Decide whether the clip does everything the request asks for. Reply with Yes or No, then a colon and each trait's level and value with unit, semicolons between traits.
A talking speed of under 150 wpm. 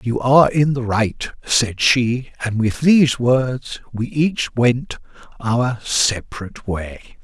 Yes: average, 140 wpm